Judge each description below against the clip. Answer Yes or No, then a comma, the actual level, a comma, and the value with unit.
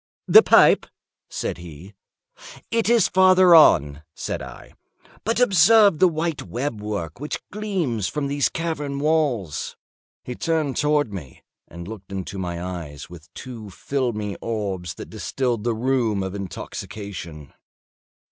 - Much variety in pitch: Yes, wide, 8.8 semitones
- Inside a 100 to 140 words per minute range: Yes, slow, 135 wpm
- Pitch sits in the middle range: No, low, 120 Hz